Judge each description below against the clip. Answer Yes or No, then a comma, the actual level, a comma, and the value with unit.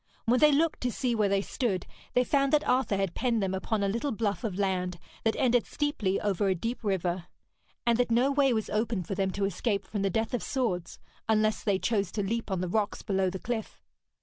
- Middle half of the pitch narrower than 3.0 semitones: No, average, 4.0 semitones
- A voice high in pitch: Yes, high, 215 Hz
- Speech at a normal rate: No, fast, 230 wpm